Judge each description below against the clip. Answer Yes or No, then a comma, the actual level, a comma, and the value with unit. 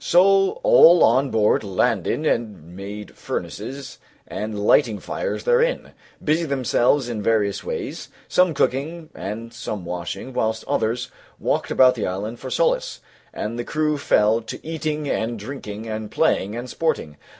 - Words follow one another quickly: No, average, 150 wpm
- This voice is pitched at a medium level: No, low, 120 Hz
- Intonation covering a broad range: Yes, wide, 6.4 semitones